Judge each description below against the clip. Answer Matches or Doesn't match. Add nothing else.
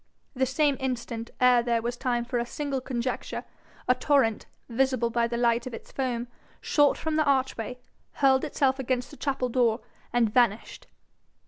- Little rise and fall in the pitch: Matches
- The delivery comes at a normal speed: Matches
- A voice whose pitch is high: Matches